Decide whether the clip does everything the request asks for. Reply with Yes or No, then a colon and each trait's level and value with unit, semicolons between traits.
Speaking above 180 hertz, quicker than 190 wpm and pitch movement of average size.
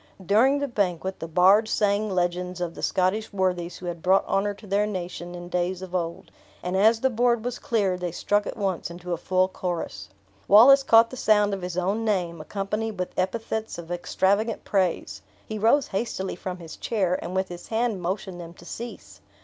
Yes: high, 190 Hz; average, 200 wpm; average, 3.4 semitones